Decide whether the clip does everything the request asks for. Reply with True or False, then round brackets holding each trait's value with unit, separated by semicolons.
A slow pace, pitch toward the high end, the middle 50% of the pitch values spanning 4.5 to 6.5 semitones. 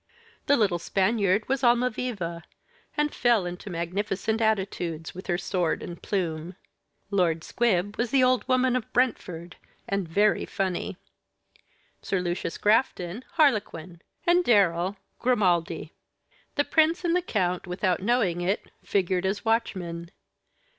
True (125 wpm; 195 Hz; 5.3 semitones)